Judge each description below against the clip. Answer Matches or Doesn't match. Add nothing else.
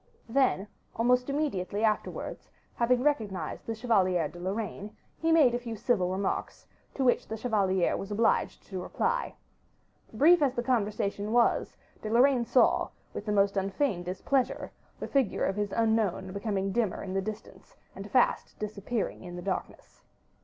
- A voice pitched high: Matches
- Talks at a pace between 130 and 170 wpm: Matches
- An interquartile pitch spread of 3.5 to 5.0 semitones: Matches